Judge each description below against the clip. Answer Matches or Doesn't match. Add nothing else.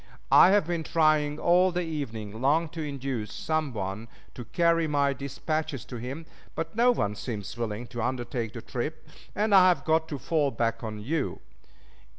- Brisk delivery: Doesn't match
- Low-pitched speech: Doesn't match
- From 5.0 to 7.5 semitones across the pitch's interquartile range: Matches